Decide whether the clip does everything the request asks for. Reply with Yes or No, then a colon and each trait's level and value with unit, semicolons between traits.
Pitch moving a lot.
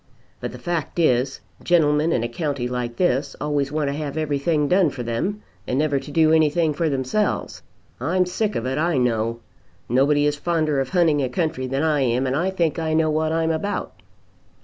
No: average, 3.5 semitones